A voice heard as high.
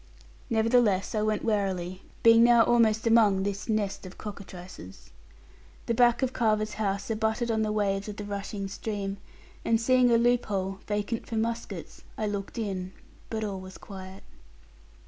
Yes: high, 210 Hz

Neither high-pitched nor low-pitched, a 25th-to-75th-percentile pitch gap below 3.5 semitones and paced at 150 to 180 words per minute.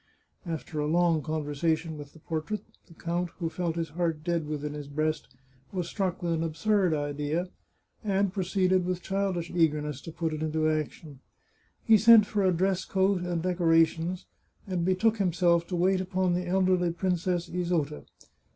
Yes: medium, 170 Hz; average, 2.8 semitones; average, 170 wpm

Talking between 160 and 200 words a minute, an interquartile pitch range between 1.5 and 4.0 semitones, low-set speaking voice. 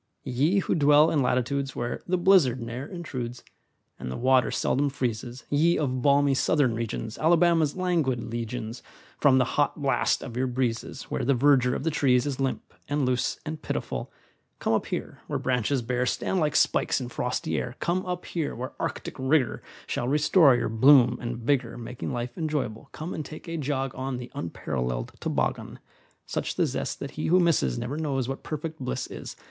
Yes: average, 185 wpm; average, 3.6 semitones; low, 130 Hz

